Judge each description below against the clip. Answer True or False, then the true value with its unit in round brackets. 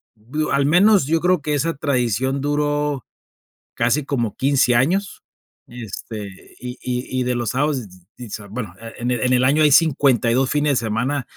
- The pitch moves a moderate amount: True (3.6 semitones)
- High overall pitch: False (130 Hz)